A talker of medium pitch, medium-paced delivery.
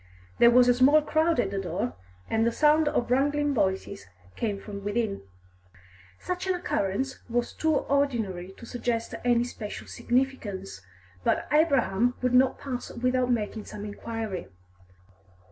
No: high, 240 Hz; average, 145 wpm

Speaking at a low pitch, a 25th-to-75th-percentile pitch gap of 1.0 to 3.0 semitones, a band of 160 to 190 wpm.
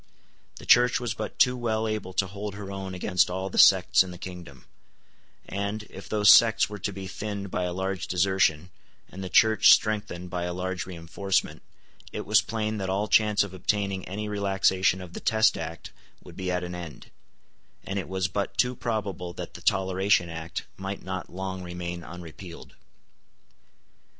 Yes: very low, 95 Hz; narrow, 2.5 semitones; average, 180 wpm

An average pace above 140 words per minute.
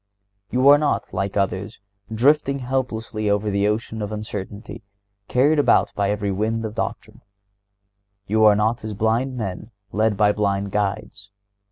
Yes: average, 160 wpm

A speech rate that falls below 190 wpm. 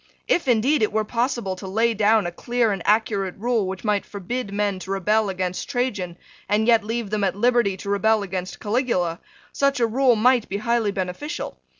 No: average, 195 wpm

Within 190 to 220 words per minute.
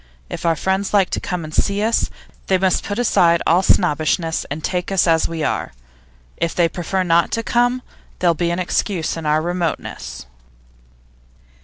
No: average, 175 wpm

